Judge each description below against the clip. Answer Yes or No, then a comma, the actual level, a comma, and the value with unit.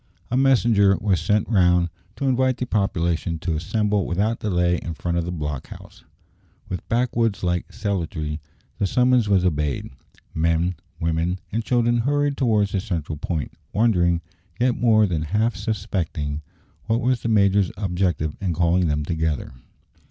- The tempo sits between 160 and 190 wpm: No, average, 150 wpm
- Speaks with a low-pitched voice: Yes, very low, 95 Hz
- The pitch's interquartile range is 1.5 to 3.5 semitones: No, average, 5.1 semitones